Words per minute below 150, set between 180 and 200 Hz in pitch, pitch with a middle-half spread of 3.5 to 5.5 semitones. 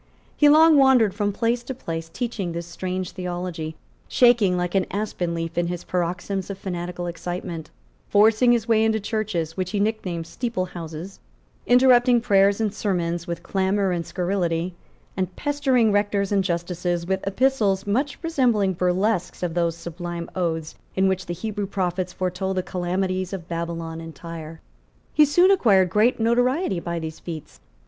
No: average, 160 wpm; medium, 185 Hz; average, 4.0 semitones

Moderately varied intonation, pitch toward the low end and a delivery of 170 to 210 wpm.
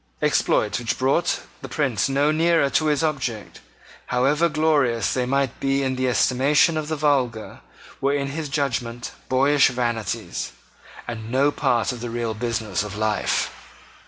No: average, 3.6 semitones; low, 130 Hz; average, 155 wpm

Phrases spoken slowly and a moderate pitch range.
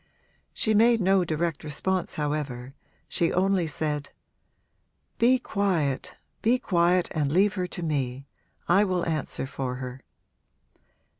Yes: slow, 125 wpm; average, 4.8 semitones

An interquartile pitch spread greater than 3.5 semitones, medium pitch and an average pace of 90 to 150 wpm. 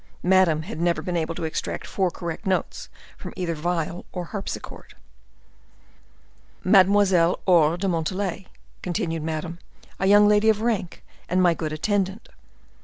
No: average, 2.8 semitones; medium, 180 Hz; average, 140 wpm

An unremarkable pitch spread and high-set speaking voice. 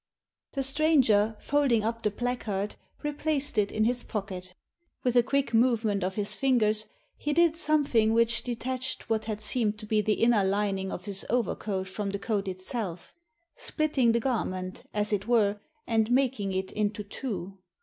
Yes: average, 3.7 semitones; high, 220 Hz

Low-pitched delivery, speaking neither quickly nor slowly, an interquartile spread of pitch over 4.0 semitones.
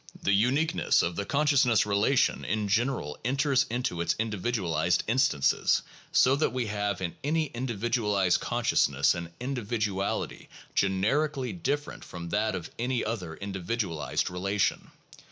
No: low, 110 Hz; slow, 130 wpm; average, 5.2 semitones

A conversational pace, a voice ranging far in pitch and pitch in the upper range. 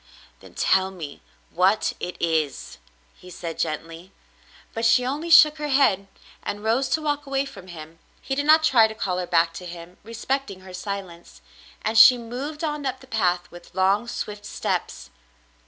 Yes: average, 175 wpm; wide, 7.2 semitones; high, 205 Hz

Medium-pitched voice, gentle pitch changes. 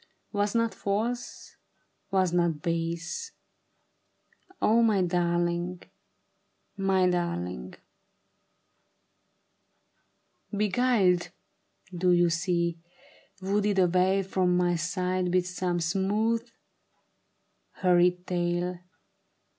Yes: medium, 180 Hz; narrow, 2.2 semitones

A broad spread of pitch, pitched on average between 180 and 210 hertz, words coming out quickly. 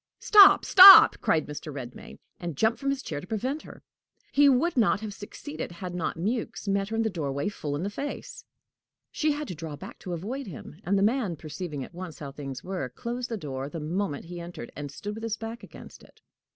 Yes: wide, 7.2 semitones; medium, 185 Hz; fast, 220 wpm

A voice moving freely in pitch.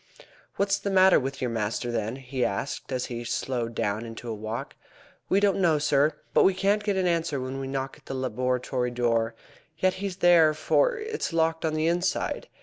Yes: wide, 6.9 semitones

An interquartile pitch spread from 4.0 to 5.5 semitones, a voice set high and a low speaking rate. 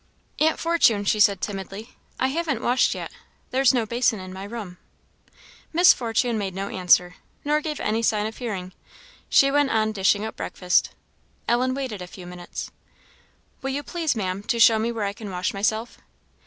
No: average, 4.7 semitones; high, 220 Hz; average, 180 wpm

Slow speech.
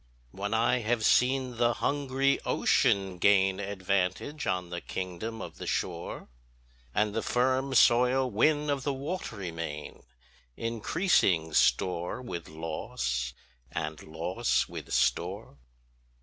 Yes: slow, 120 wpm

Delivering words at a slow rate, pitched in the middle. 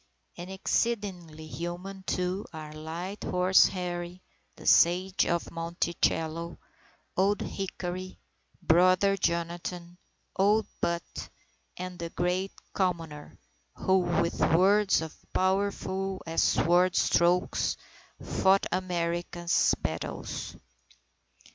Yes: slow, 90 wpm; medium, 180 Hz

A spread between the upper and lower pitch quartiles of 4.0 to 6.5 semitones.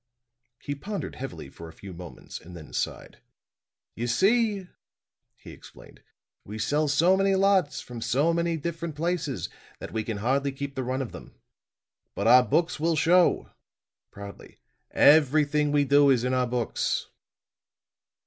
Yes: wide, 5.5 semitones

